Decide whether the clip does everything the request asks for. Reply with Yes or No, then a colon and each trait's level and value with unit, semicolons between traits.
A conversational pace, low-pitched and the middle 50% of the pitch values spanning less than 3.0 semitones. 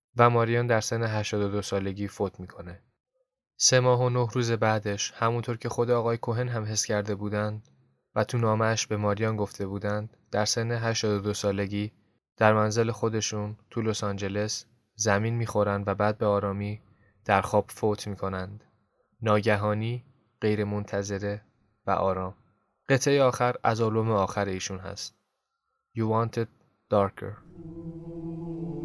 Yes: average, 135 wpm; low, 110 Hz; narrow, 2.6 semitones